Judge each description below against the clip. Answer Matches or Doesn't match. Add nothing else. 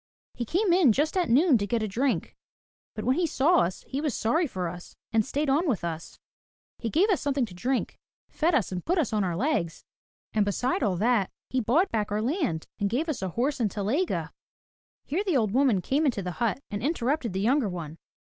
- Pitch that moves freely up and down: Matches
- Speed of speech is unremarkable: Doesn't match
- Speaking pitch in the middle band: Doesn't match